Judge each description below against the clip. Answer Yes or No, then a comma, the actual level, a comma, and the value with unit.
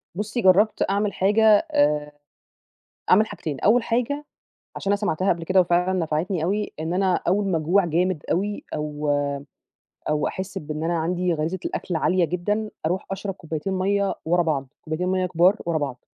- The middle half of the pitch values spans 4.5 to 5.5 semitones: No, average, 3.8 semitones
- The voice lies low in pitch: No, medium, 180 Hz